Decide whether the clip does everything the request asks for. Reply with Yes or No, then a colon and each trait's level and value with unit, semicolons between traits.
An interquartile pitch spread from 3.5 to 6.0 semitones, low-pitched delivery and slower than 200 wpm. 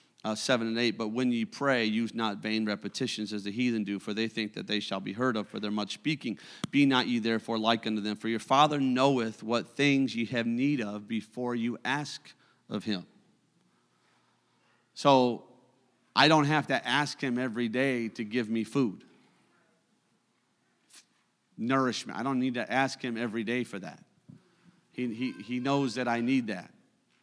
No: average, 3.0 semitones; low, 120 Hz; average, 185 wpm